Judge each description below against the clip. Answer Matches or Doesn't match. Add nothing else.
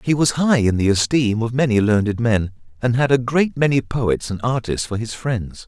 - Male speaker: Matches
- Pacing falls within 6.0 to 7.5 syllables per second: Doesn't match